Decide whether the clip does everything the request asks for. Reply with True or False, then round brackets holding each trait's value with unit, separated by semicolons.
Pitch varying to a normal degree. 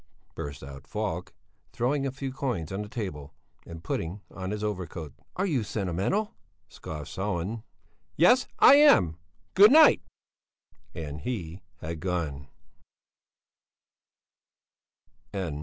False (7.7 semitones)